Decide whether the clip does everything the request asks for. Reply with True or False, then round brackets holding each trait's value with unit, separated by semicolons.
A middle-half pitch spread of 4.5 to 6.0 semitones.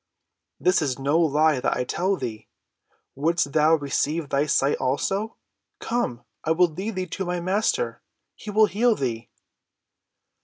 True (5.4 semitones)